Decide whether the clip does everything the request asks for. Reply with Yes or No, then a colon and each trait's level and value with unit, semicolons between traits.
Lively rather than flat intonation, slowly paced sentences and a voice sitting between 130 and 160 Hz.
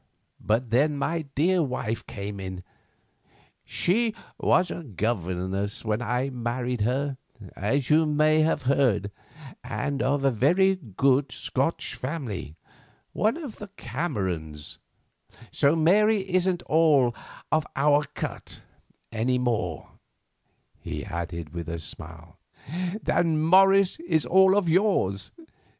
Yes: wide, 7.8 semitones; slow, 115 wpm; low, 135 Hz